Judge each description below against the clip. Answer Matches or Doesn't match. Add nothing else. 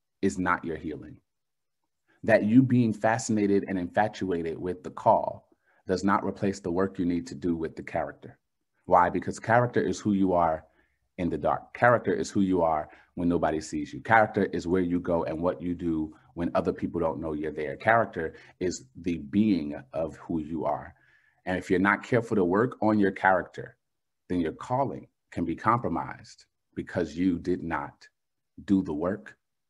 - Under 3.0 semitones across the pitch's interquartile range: Matches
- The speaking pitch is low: Matches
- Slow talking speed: Doesn't match